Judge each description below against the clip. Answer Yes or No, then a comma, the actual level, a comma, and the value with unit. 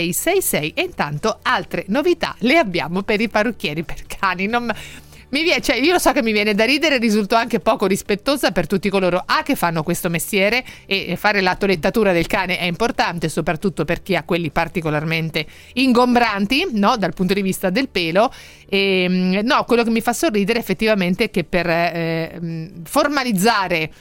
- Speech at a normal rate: No, fast, 180 wpm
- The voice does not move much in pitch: No, average, 5.1 semitones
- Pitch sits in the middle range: No, high, 200 Hz